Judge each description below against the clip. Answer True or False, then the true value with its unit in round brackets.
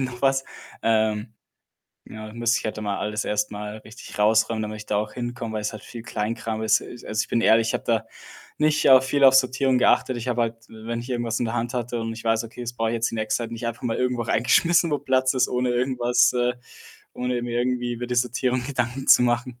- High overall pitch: False (120 Hz)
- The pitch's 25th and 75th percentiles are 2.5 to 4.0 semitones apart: False (2.0 semitones)